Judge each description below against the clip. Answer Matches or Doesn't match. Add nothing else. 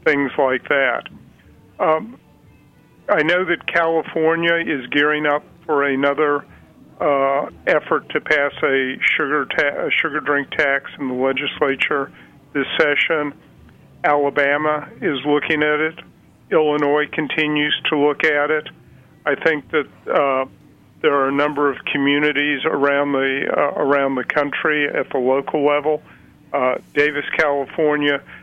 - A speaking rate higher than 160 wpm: Doesn't match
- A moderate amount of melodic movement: Doesn't match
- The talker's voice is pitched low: Doesn't match